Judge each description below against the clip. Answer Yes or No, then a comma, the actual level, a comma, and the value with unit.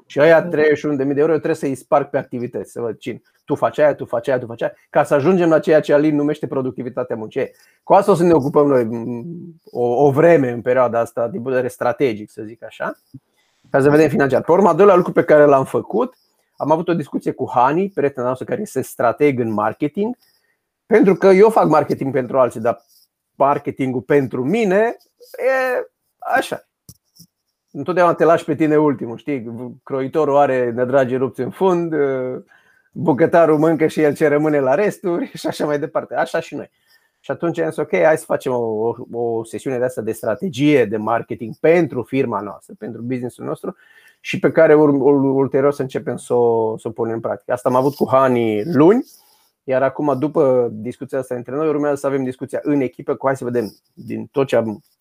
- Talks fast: Yes, fast, 200 wpm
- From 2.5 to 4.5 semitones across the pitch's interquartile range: Yes, average, 4.0 semitones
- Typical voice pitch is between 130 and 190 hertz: Yes, medium, 140 Hz